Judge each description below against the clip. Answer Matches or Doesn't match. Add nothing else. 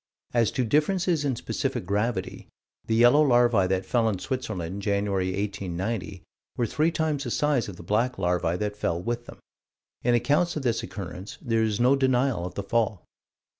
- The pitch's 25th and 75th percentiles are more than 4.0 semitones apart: Matches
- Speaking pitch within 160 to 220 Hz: Doesn't match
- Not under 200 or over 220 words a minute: Doesn't match